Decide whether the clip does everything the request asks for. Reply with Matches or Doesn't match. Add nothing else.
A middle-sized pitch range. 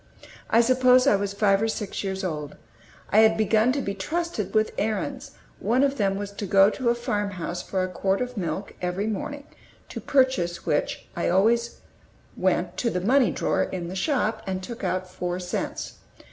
Matches